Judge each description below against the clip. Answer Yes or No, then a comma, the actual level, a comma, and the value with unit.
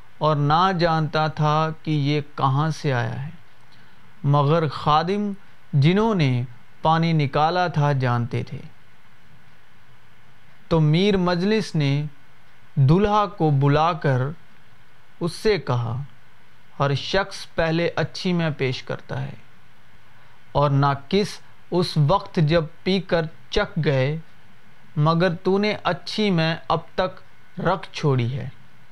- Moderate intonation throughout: Yes, average, 4.2 semitones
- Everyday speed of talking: Yes, average, 120 wpm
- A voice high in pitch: No, medium, 150 Hz